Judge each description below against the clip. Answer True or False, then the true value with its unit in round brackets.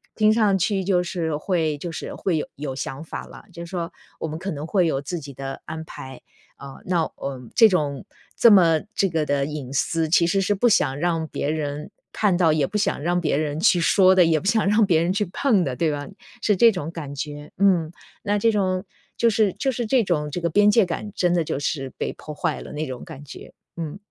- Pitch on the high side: False (165 Hz)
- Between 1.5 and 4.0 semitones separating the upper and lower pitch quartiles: False (4.6 semitones)